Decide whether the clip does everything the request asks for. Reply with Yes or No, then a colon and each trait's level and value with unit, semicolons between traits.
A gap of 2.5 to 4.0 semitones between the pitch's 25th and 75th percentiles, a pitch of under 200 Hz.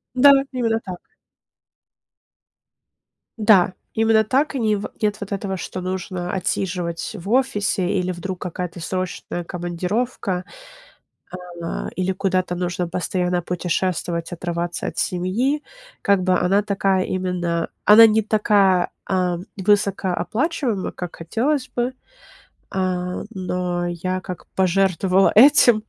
Yes: average, 2.9 semitones; medium, 185 Hz